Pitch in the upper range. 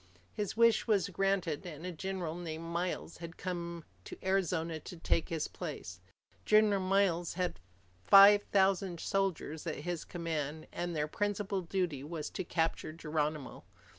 No: medium, 175 Hz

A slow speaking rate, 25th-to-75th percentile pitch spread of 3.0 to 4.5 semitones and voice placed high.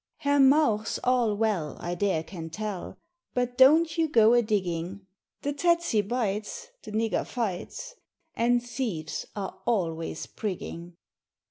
No: slow, 130 wpm; wide, 5.5 semitones; high, 220 Hz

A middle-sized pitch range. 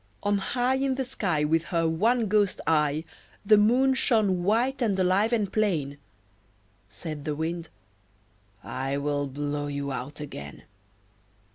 No: wide, 6.8 semitones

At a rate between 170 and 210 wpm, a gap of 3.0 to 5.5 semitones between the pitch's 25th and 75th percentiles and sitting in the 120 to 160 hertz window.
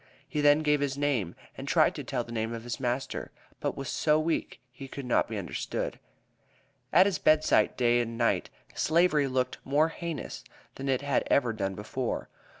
Yes: average, 185 wpm; average, 4.0 semitones; low, 135 Hz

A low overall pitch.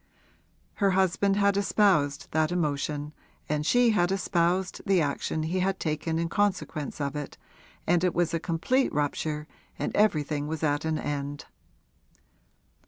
No: medium, 165 Hz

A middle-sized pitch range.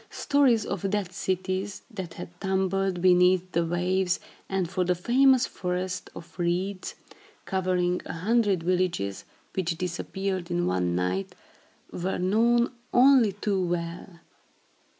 No: narrow, 2.0 semitones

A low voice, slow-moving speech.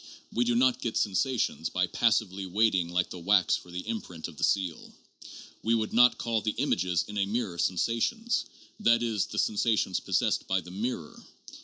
No: low, 105 Hz; average, 180 wpm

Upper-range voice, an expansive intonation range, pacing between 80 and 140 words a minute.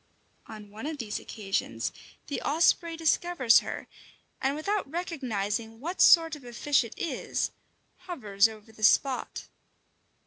Yes: very high, 265 Hz; wide, 6.9 semitones; slow, 135 wpm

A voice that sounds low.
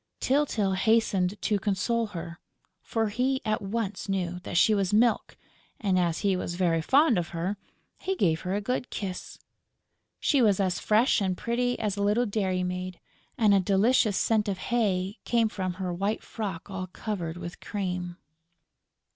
No: high, 200 Hz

